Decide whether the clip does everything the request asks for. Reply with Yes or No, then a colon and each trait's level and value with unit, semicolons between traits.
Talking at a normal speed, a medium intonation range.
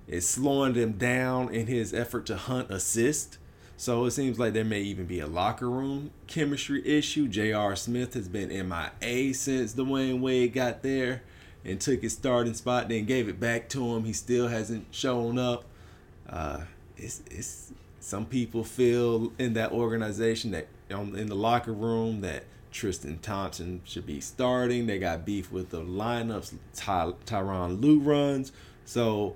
Yes: average, 170 wpm; average, 4.5 semitones